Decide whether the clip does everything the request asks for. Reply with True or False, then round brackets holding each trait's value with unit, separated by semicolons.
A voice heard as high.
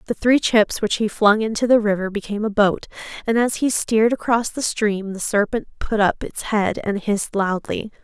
True (215 Hz)